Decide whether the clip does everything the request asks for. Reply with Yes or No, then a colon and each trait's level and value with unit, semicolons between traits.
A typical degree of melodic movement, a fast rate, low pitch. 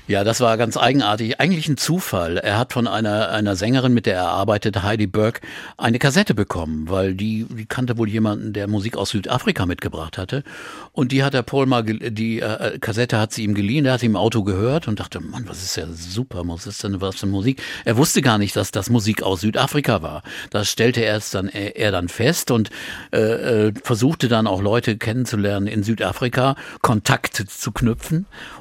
Yes: average, 3.3 semitones; fast, 210 wpm; low, 110 Hz